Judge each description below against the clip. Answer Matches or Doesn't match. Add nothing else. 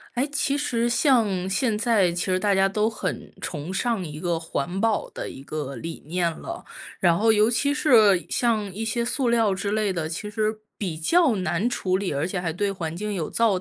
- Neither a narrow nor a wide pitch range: Matches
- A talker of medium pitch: Doesn't match